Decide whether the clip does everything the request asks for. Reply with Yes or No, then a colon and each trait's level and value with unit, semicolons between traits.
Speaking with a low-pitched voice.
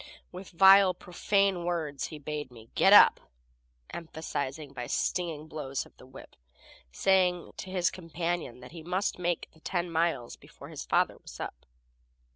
No: medium, 165 Hz